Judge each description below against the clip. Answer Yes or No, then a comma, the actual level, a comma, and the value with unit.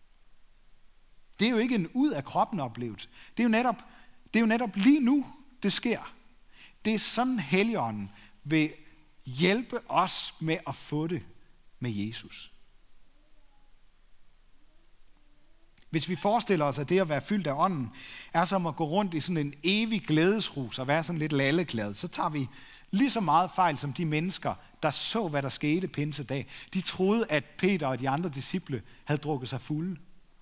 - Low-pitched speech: No, medium, 165 Hz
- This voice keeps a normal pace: Yes, average, 175 wpm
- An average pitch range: No, wide, 6.5 semitones